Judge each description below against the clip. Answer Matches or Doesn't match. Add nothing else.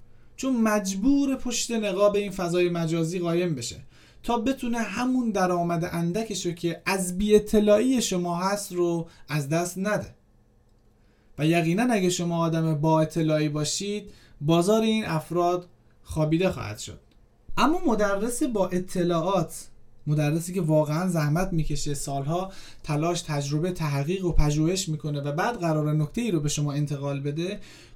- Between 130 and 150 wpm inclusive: Matches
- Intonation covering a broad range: Doesn't match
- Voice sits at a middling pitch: Matches